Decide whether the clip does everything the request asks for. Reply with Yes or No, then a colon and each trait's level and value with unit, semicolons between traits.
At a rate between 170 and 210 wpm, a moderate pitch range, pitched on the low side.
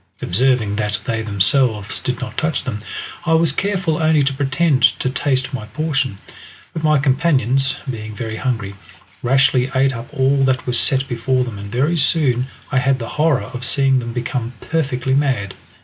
Yes: average, 175 wpm; average, 3.1 semitones; low, 130 Hz